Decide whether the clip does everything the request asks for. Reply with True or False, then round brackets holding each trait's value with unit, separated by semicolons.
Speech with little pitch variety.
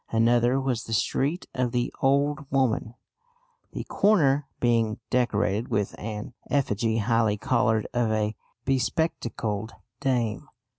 False (3.4 semitones)